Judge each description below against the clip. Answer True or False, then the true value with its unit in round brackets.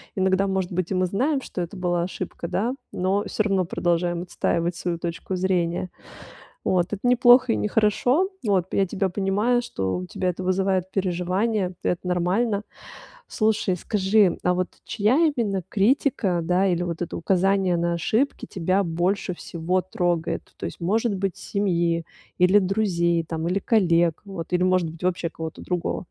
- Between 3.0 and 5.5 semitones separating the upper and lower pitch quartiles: False (2.4 semitones)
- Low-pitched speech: False (185 Hz)